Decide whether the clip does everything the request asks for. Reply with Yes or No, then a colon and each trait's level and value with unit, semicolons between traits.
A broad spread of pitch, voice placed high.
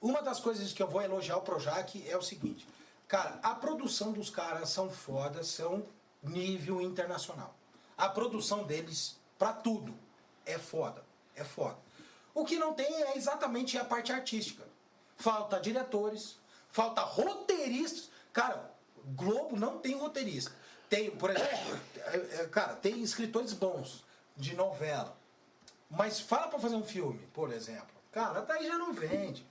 Yes: wide, 5.9 semitones; high, 215 Hz